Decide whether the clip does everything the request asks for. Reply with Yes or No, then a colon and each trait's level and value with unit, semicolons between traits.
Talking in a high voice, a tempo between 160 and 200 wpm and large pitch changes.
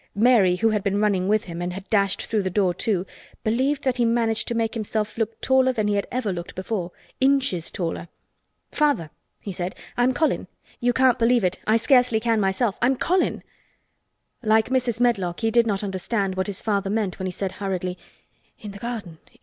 No: high, 215 Hz; average, 195 wpm; average, 4.0 semitones